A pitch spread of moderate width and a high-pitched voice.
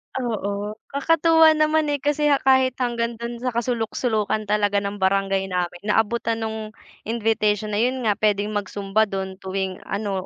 Yes: average, 3.4 semitones; high, 215 Hz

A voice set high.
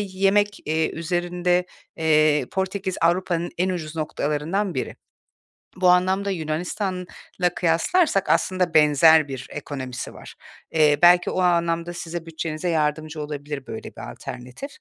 No: medium, 170 Hz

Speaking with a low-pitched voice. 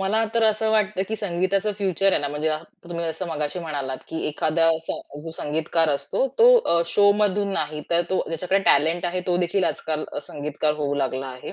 No: medium, 170 Hz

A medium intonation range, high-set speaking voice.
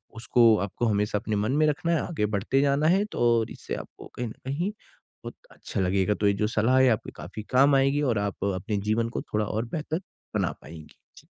No: average, 4.8 semitones; low, 115 Hz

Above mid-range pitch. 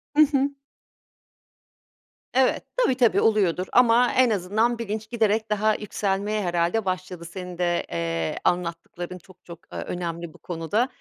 Yes: high, 195 Hz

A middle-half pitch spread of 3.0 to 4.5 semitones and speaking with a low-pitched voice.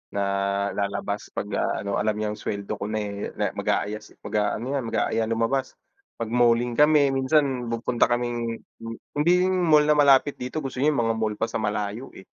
Yes: average, 4.1 semitones; low, 115 Hz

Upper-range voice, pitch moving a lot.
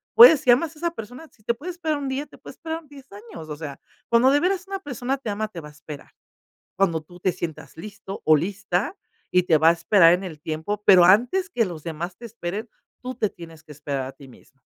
Yes: high, 205 Hz; wide, 8.5 semitones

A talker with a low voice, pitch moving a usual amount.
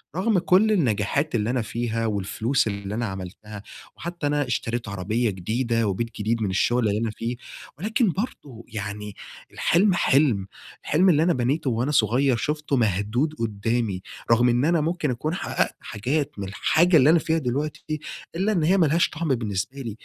No: low, 120 Hz; wide, 6.3 semitones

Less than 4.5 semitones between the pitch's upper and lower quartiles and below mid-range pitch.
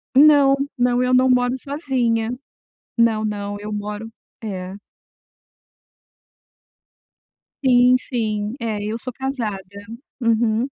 No: average, 3.1 semitones; high, 230 Hz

